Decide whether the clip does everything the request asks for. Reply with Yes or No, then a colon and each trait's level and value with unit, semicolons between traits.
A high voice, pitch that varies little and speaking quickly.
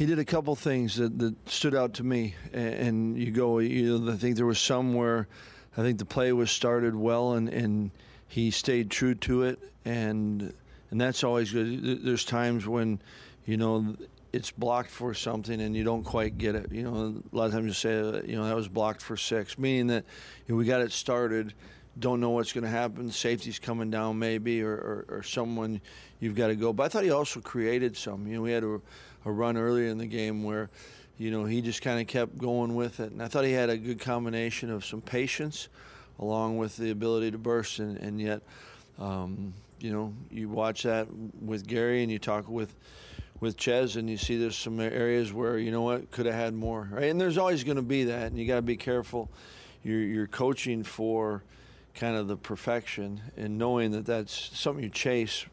No: low, 115 Hz; narrow, 1.8 semitones; fast, 220 wpm